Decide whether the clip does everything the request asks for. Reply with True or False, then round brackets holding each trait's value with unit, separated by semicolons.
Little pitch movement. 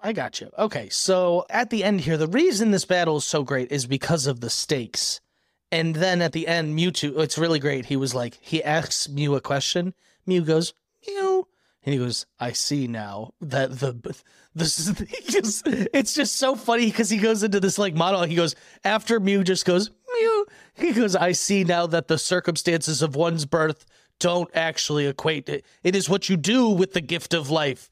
False (4.8 semitones)